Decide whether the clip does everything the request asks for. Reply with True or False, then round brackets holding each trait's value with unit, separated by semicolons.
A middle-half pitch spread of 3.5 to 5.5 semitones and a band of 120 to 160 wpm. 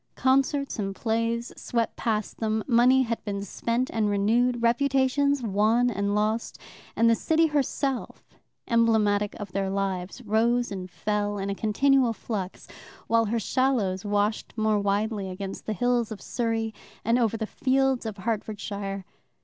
False (3.0 semitones; 150 wpm)